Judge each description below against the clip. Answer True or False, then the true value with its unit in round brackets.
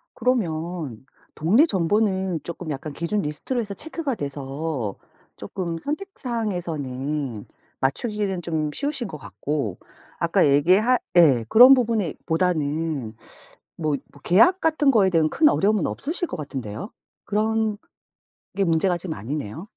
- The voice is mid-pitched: True (175 Hz)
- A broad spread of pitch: True (6.8 semitones)